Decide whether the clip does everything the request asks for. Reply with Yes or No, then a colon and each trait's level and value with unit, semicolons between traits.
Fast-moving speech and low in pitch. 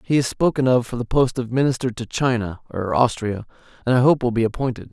Yes: fast, 230 wpm; low, 125 Hz